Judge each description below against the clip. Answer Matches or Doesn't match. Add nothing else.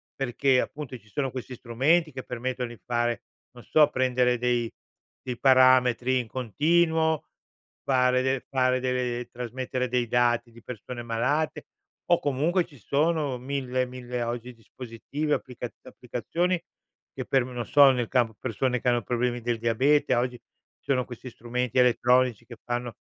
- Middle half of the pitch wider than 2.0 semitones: Doesn't match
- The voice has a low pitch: Matches